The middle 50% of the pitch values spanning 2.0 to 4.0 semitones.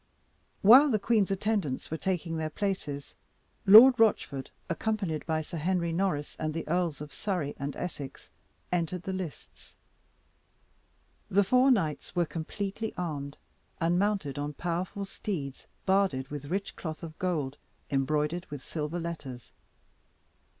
No: average, 4.6 semitones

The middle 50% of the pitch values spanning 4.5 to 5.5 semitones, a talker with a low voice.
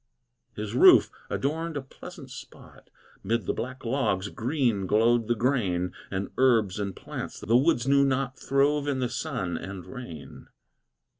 Yes: average, 5.2 semitones; low, 120 Hz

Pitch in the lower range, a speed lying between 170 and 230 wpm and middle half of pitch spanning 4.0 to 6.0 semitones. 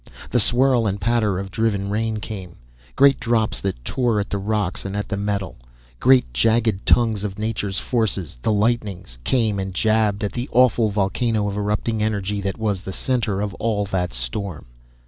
No: low, 105 Hz; average, 180 wpm; narrow, 2.5 semitones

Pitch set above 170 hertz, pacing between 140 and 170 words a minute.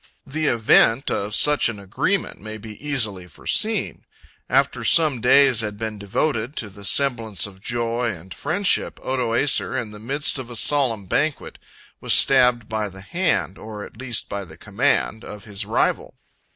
No: low, 115 Hz; average, 165 wpm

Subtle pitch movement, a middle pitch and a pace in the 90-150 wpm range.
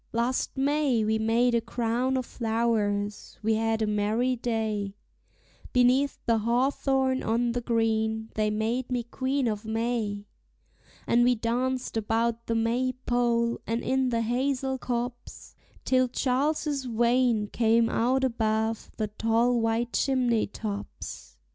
No: narrow, 2.2 semitones; high, 235 Hz; slow, 135 wpm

